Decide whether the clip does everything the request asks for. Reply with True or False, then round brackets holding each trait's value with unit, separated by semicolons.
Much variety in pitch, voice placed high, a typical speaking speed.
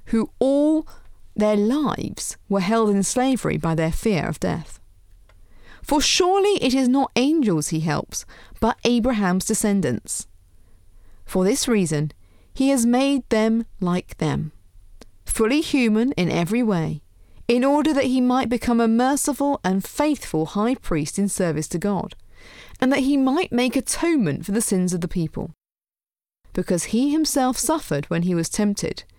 True (7.7 semitones; 220 Hz; 150 wpm)